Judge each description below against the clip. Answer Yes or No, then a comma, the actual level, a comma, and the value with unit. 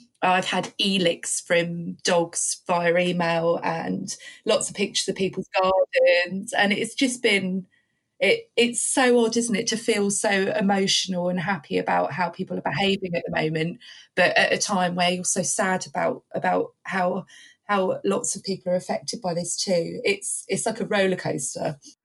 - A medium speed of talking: Yes, average, 170 wpm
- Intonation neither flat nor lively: Yes, average, 3.4 semitones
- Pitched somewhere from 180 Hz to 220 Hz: Yes, high, 190 Hz